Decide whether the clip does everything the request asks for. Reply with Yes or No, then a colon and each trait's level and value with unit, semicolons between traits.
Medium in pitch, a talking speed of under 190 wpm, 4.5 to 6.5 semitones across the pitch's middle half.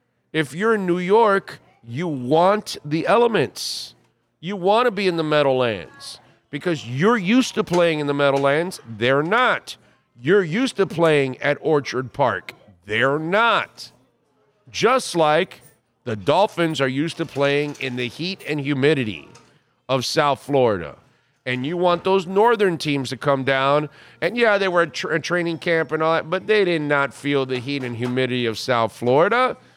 Yes: medium, 150 Hz; average, 165 wpm; average, 5.3 semitones